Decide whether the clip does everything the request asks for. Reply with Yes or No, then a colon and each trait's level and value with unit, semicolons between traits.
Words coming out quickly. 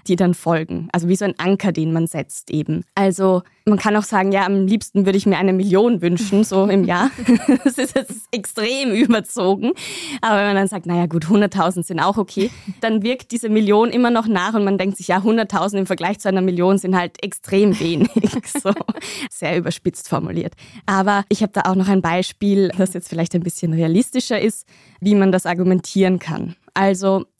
Yes: fast, 200 wpm